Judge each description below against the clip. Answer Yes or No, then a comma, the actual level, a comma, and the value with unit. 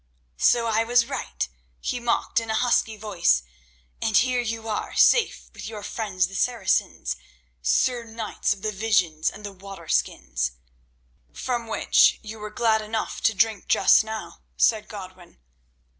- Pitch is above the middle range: Yes, high, 215 Hz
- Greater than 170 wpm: No, average, 155 wpm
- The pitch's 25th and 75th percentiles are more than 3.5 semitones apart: No, average, 3.0 semitones